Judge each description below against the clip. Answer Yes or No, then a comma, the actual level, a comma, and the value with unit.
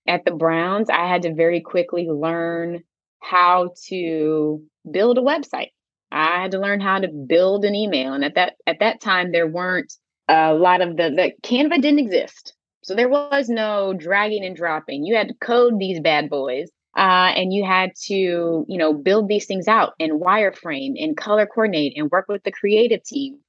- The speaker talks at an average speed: Yes, average, 190 wpm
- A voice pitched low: No, medium, 185 Hz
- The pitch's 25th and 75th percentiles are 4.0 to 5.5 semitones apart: Yes, average, 4.3 semitones